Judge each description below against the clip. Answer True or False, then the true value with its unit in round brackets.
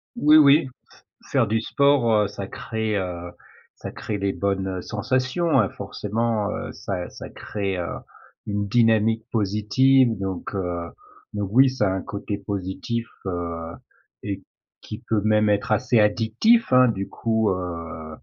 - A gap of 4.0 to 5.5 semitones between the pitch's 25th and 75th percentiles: False (3.3 semitones)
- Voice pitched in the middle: False (105 Hz)